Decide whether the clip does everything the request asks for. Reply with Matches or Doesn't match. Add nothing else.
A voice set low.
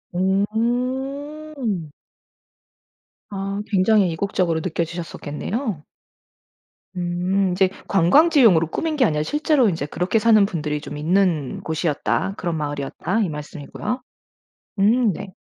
Doesn't match